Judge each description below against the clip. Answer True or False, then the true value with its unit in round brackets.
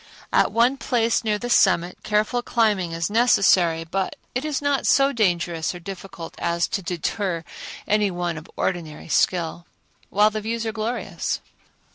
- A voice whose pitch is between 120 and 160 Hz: False (195 Hz)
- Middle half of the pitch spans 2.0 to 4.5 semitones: False (4.9 semitones)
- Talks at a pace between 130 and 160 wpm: True (155 wpm)